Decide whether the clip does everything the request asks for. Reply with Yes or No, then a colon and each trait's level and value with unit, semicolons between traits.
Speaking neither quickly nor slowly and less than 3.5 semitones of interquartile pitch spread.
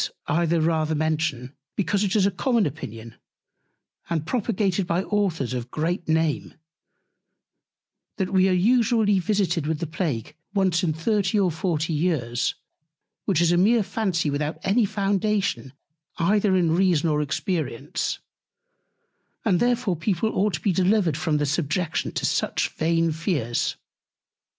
No: average, 145 wpm; average, 4.0 semitones